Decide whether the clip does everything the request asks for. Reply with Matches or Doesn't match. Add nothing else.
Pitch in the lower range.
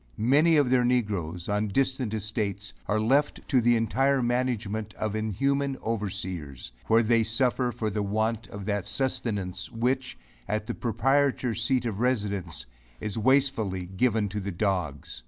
Matches